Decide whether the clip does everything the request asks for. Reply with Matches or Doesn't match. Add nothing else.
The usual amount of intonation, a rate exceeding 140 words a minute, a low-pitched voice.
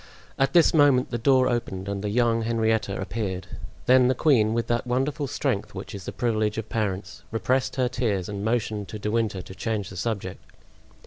Matches